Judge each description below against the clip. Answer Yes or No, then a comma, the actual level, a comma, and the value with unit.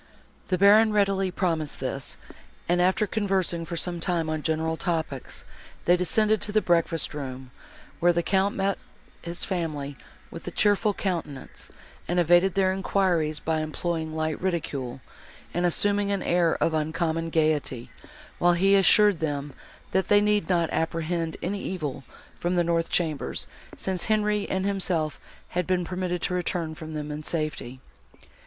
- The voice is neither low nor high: Yes, medium, 175 Hz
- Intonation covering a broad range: No, average, 3.3 semitones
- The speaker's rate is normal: Yes, average, 155 wpm